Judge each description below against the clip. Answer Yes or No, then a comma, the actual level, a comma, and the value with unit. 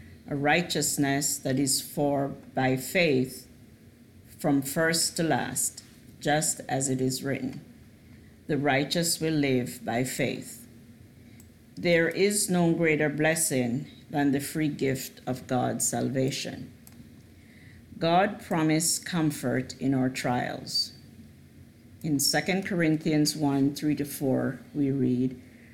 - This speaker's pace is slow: Yes, slow, 115 wpm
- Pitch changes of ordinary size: Yes, average, 3.7 semitones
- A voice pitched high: No, medium, 140 Hz